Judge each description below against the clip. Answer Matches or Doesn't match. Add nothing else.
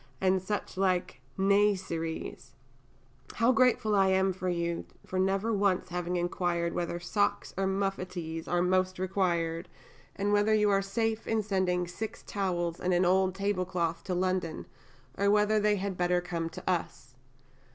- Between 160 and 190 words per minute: Doesn't match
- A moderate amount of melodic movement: Doesn't match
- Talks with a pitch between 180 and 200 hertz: Matches